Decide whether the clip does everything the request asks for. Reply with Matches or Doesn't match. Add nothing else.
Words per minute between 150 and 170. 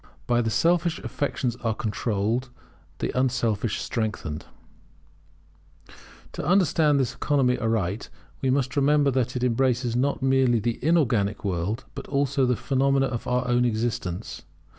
Doesn't match